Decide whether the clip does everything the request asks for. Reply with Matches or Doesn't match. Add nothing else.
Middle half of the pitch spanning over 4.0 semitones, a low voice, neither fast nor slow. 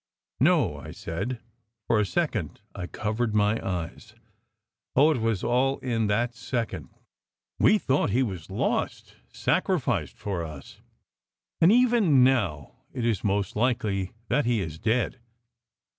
Matches